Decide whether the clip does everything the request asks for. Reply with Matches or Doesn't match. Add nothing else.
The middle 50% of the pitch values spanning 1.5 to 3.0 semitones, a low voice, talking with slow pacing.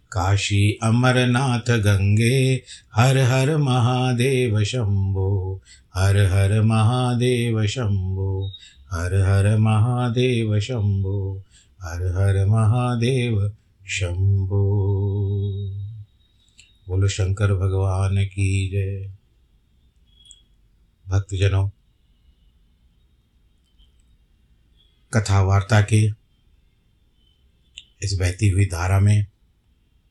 Matches